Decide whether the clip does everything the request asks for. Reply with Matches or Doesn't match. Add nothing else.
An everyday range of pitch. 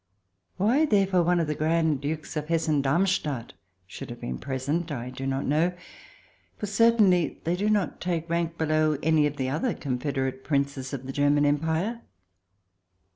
Matches